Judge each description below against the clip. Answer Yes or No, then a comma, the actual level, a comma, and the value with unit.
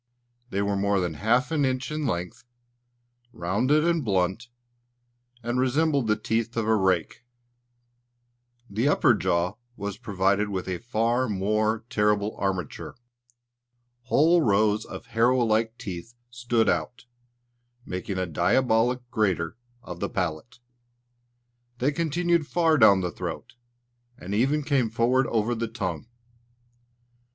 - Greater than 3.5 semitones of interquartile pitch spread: Yes, average, 4.4 semitones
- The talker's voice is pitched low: Yes, low, 110 Hz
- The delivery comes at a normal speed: No, slow, 125 wpm